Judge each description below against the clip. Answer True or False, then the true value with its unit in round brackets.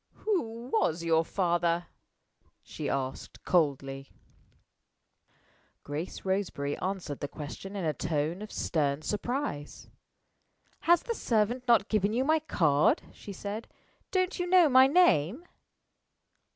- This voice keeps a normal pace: False (120 wpm)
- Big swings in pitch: True (8.4 semitones)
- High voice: True (195 Hz)